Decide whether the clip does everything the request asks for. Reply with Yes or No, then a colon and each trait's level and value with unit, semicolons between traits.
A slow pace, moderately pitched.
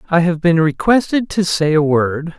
No: average, 200 wpm; medium, 170 Hz